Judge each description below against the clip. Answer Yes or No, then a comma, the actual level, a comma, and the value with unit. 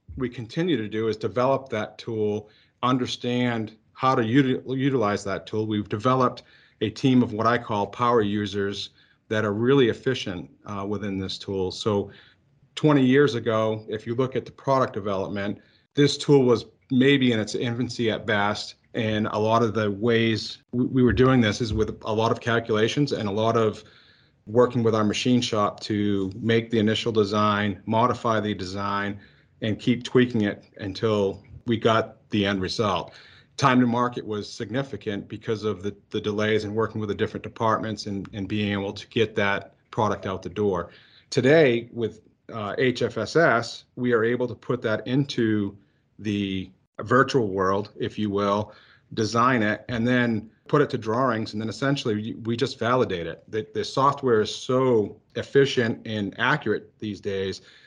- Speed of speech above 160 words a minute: Yes, average, 170 wpm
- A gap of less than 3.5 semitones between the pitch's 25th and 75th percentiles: Yes, average, 3.0 semitones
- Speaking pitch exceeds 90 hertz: Yes, low, 110 Hz